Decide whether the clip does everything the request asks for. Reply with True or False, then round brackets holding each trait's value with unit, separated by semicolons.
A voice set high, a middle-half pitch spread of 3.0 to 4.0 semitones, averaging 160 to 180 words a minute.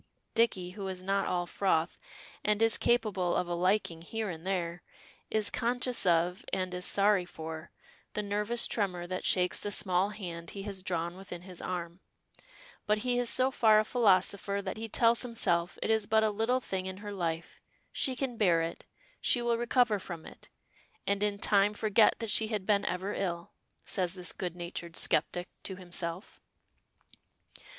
True (195 Hz; 3.4 semitones; 175 wpm)